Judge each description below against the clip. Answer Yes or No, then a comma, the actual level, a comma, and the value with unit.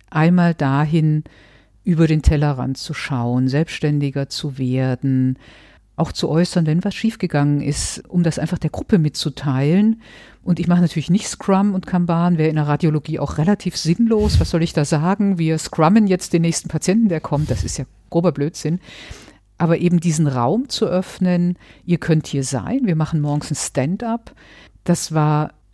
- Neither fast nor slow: Yes, average, 170 wpm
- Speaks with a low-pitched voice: No, medium, 160 Hz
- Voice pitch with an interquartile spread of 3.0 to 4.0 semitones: Yes, average, 3.5 semitones